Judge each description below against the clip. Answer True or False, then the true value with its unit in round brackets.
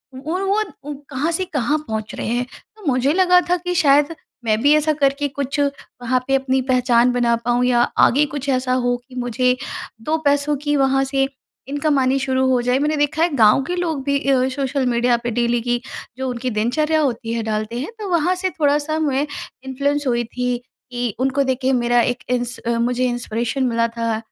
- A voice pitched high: True (260 Hz)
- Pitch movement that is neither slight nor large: True (3.1 semitones)